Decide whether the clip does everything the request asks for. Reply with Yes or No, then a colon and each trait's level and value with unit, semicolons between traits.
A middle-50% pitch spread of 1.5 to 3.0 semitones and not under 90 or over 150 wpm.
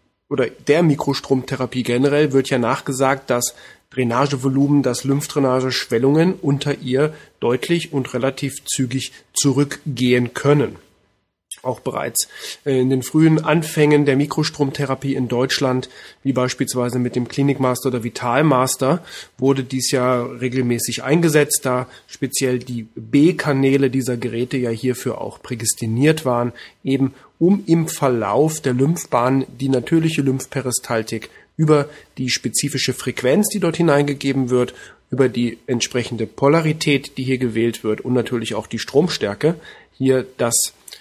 Yes: narrow, 2.4 semitones; slow, 125 wpm